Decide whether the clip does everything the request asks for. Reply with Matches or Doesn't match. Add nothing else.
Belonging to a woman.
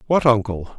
Doesn't match